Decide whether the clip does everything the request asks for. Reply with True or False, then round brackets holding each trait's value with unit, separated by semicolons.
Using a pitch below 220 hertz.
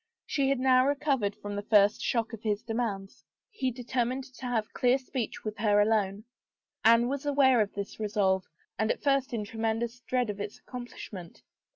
False (230 Hz)